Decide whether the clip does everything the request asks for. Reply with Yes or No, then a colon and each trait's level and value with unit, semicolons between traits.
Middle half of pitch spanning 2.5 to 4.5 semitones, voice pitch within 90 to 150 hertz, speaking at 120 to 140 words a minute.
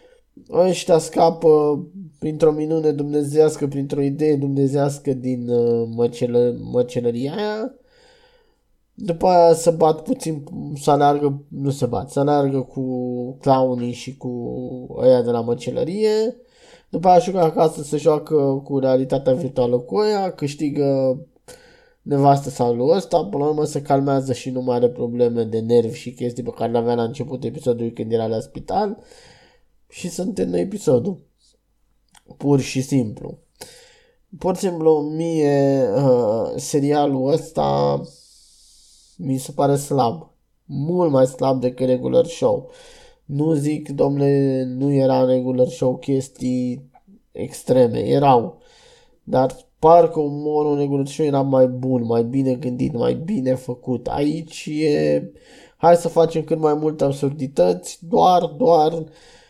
Yes: average, 4.2 semitones; medium, 140 Hz; average, 135 wpm